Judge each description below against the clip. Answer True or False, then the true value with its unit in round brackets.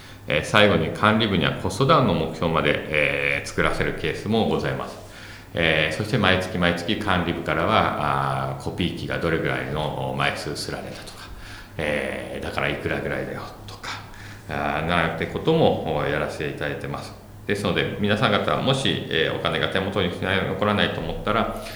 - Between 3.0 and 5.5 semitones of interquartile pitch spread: True (5.2 semitones)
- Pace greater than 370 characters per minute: False (345 characters per minute)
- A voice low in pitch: True (90 Hz)